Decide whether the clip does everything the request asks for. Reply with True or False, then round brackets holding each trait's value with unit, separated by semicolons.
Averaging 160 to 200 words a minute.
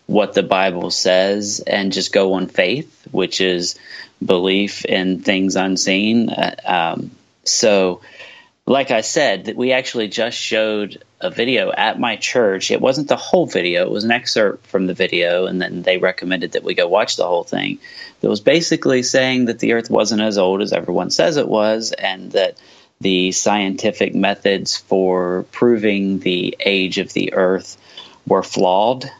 True (170 wpm)